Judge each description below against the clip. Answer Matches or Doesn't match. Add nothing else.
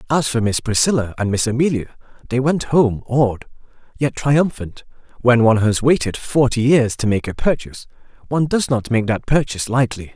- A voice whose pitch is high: Doesn't match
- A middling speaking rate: Matches